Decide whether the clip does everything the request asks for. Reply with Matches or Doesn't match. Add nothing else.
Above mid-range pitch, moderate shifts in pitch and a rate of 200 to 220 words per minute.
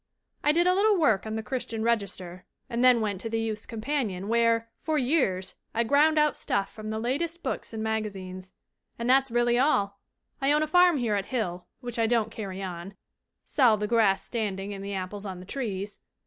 Matches